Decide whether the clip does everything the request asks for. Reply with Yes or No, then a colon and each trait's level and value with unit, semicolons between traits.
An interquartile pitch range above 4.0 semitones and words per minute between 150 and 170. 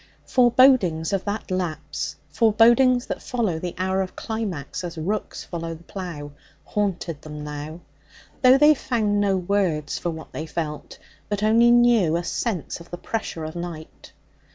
Yes: wide, 5.5 semitones; average, 155 wpm